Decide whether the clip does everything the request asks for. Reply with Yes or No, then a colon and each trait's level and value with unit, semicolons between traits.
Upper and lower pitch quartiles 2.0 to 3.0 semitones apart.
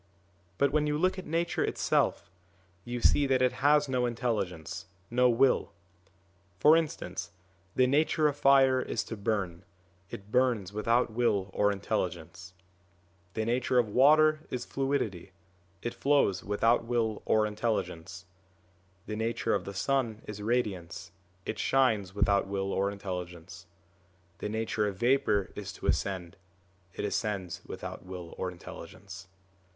No: average, 5.1 semitones